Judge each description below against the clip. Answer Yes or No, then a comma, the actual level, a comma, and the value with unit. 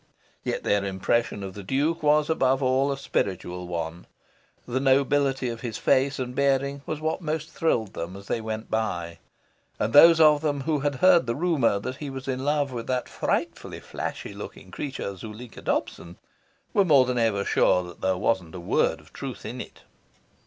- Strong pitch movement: Yes, wide, 6.0 semitones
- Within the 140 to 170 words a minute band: No, average, 185 wpm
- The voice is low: Yes, low, 130 Hz